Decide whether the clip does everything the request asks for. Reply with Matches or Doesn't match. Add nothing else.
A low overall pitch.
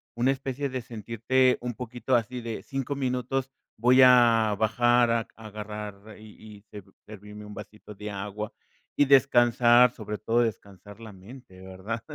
Matches